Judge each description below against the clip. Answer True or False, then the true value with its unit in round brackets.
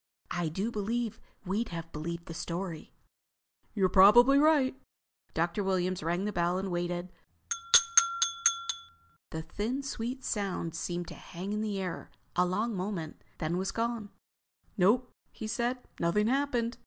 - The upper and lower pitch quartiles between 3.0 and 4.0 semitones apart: False (4.8 semitones)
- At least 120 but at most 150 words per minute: True (140 wpm)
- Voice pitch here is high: True (195 Hz)